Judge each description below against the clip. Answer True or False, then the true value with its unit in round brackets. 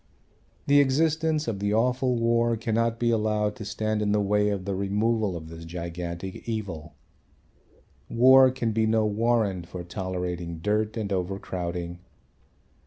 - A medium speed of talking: True (145 wpm)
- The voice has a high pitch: False (105 Hz)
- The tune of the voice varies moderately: True (4.1 semitones)